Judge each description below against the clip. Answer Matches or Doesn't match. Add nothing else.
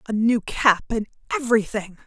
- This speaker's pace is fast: Doesn't match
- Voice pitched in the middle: Doesn't match